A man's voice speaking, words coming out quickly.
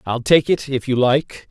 Yes: male; fast, 240 wpm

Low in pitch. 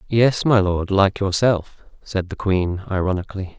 Yes: low, 100 Hz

